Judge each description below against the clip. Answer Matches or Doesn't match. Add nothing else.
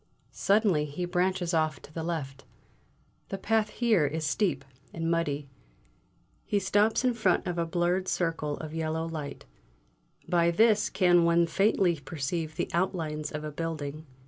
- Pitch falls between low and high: Matches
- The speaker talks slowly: Doesn't match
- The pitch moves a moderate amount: Matches